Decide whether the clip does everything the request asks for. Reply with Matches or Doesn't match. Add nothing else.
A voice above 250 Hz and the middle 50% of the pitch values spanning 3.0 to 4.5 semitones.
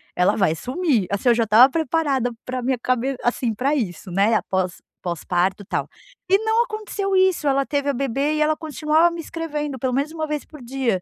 Doesn't match